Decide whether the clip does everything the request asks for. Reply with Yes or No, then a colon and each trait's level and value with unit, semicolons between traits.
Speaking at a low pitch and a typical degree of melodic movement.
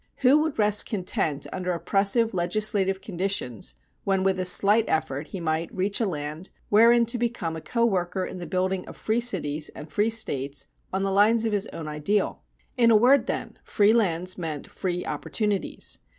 No: high, 195 Hz; average, 4.3 semitones